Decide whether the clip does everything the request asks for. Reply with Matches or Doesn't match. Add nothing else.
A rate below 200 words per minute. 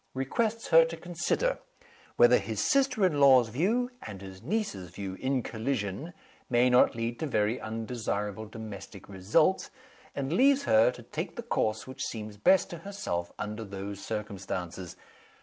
Matches